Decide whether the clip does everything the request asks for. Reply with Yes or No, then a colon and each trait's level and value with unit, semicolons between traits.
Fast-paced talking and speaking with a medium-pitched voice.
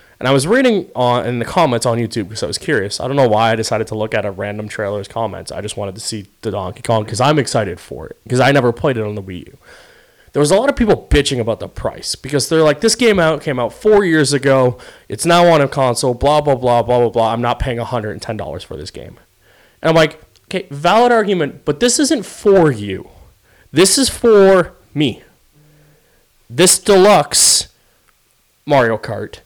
No: fast, 220 wpm; low, 130 Hz